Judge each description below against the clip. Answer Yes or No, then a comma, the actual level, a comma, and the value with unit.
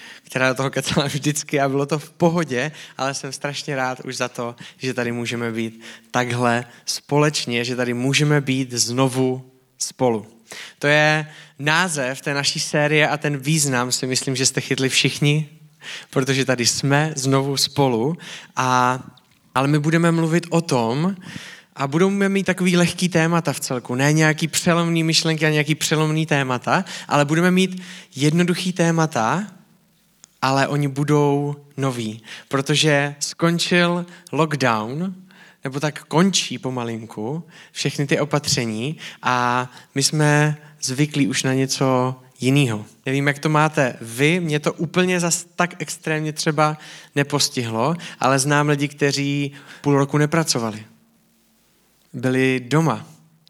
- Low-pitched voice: No, medium, 145 Hz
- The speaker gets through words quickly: No, average, 135 wpm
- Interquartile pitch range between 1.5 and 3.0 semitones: No, average, 3.7 semitones